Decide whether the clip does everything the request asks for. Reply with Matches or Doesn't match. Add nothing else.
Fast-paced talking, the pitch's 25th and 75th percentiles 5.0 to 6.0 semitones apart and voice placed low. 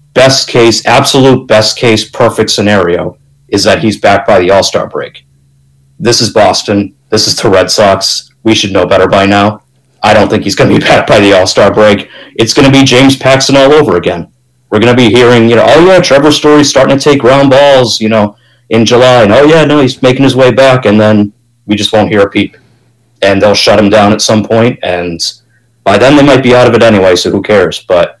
Doesn't match